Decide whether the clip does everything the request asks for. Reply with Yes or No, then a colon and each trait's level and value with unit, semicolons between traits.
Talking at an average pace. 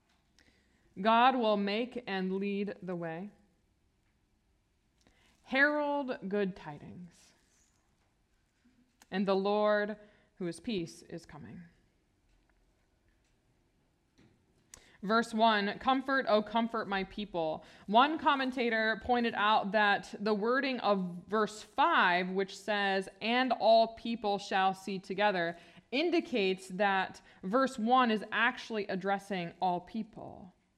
No: slow, 100 wpm